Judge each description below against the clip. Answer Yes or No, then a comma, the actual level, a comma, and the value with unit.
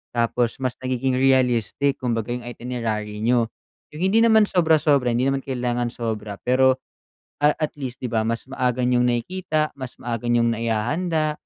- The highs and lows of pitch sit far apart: No, average, 2.8 semitones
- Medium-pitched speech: No, low, 125 Hz